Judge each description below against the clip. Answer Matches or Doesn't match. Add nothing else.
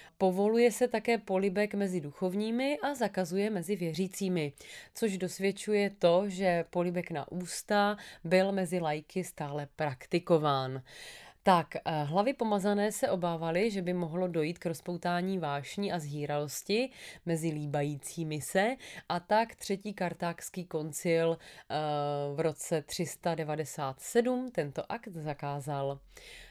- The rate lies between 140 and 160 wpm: Doesn't match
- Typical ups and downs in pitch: Matches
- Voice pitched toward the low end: Doesn't match